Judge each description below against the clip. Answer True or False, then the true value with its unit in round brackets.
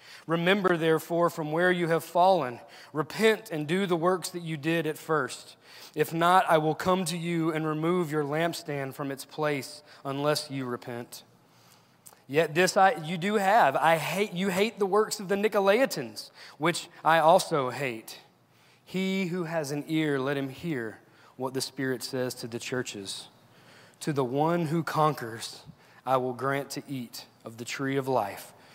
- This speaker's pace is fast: False (175 wpm)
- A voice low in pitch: False (155 Hz)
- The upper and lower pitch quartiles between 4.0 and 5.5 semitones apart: True (4.4 semitones)